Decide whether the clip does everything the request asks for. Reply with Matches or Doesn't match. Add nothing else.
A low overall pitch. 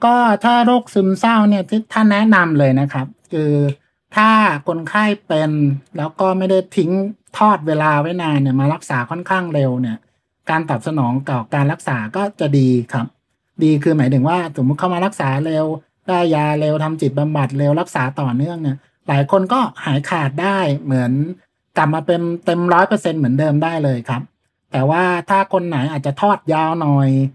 Doesn't match